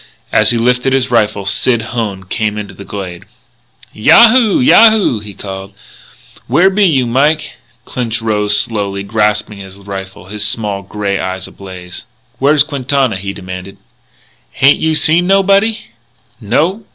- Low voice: Yes, low, 110 Hz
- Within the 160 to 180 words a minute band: No, average, 140 wpm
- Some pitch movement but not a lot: No, wide, 6.2 semitones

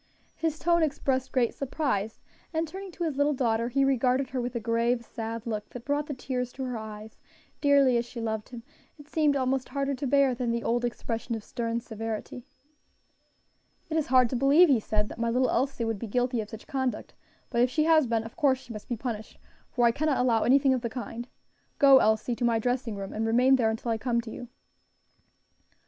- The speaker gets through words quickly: Yes, fast, 220 wpm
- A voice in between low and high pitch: No, high, 245 Hz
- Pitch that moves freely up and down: No, average, 3.0 semitones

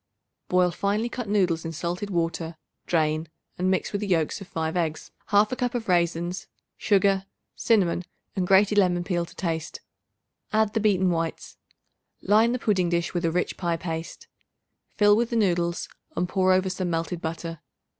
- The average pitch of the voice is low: No, medium, 180 Hz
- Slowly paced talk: No, average, 170 wpm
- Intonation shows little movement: No, average, 3.3 semitones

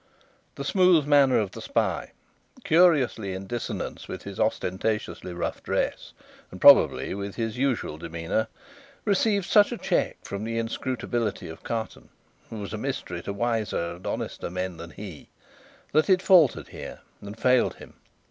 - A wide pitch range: Yes, wide, 6.6 semitones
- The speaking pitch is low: Yes, low, 110 Hz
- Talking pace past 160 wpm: No, average, 155 wpm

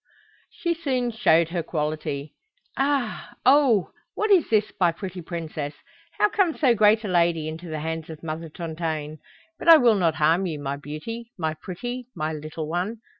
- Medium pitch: Yes, medium, 175 Hz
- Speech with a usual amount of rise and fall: No, wide, 6.9 semitones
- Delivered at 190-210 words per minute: No, average, 175 wpm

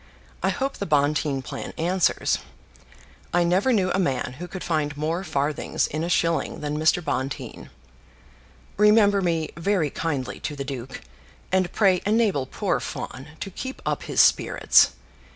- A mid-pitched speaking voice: Yes, medium, 165 Hz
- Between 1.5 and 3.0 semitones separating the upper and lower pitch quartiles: No, average, 4.7 semitones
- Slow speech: No, average, 150 wpm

